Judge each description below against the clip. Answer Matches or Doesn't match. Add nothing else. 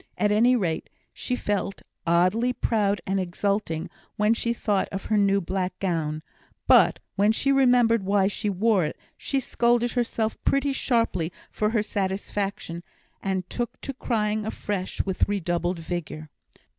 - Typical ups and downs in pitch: Matches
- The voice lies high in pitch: Matches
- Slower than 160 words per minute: Matches